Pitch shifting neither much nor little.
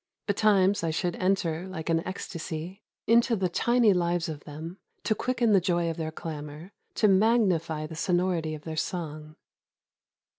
Yes: average, 3.6 semitones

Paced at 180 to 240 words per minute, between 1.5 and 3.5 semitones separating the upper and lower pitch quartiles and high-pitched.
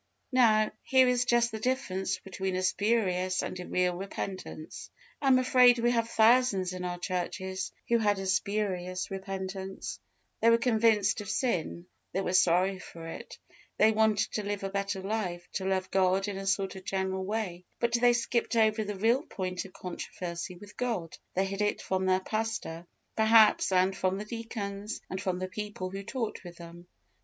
Yes: average, 185 wpm; average, 3.0 semitones; high, 195 Hz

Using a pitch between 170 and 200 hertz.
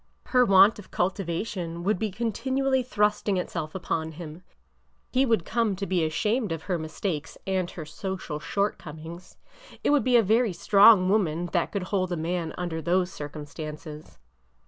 Yes: medium, 185 Hz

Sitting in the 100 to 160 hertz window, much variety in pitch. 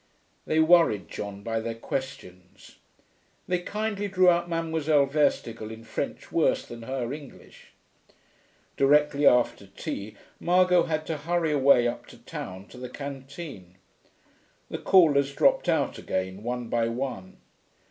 Yes: low, 135 Hz; wide, 6.0 semitones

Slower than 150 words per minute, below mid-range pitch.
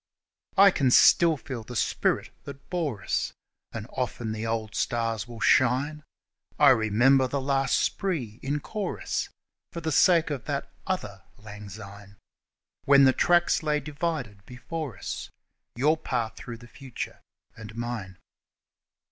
Yes: average, 140 wpm; low, 130 Hz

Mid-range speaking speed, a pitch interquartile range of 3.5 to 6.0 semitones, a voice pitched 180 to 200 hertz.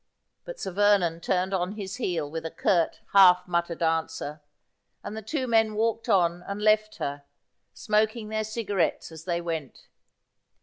Yes: average, 160 wpm; average, 4.2 semitones; high, 190 Hz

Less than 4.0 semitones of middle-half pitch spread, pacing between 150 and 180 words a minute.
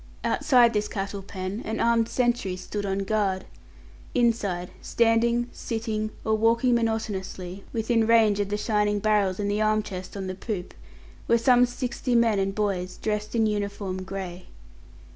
Yes: average, 2.8 semitones; average, 155 wpm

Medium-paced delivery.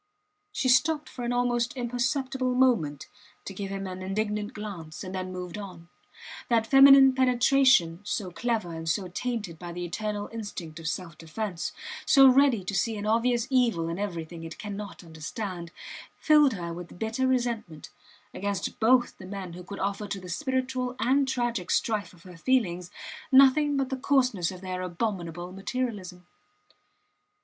Yes: average, 160 wpm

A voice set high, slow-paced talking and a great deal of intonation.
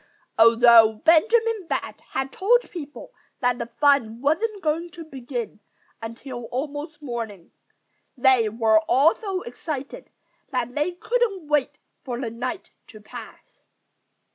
Yes: very high, 270 Hz; slow, 125 wpm; wide, 5.8 semitones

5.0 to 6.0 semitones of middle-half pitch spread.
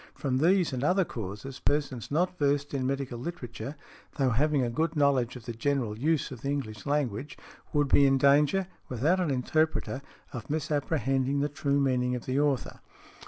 No: average, 2.7 semitones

